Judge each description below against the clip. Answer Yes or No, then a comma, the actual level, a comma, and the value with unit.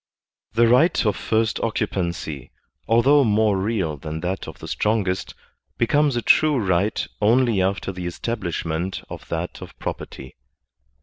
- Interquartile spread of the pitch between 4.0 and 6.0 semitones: Yes, average, 4.8 semitones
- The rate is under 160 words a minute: Yes, average, 140 wpm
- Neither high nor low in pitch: No, low, 105 Hz